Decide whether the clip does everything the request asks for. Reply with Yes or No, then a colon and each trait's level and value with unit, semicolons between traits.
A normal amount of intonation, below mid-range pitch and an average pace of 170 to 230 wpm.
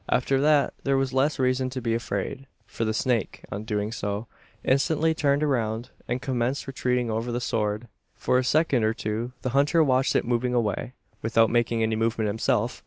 Yes: average, 3.1 semitones; low, 120 Hz; average, 185 wpm